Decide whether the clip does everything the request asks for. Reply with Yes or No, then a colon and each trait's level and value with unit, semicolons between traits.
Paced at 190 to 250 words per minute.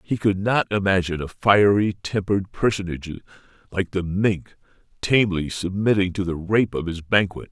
No: average, 150 wpm